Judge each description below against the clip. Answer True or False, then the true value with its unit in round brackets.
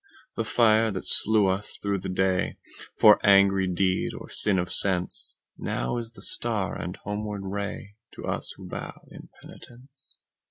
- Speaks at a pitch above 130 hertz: False (100 Hz)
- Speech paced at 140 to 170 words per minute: True (145 wpm)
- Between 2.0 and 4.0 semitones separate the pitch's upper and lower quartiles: True (2.5 semitones)